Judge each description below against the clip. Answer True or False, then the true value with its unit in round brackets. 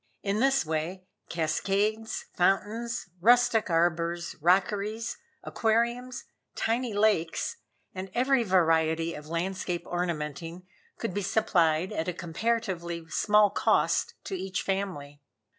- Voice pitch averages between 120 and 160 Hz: False (190 Hz)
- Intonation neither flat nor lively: True (4.8 semitones)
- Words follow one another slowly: True (110 wpm)